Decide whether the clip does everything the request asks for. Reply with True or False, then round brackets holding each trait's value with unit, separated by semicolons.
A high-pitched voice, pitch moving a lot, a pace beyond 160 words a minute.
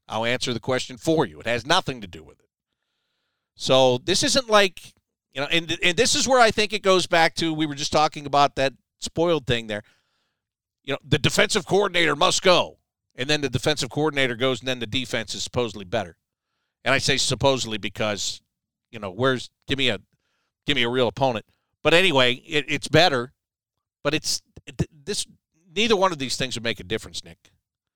False (135 Hz; 5.8 semitones; 200 wpm)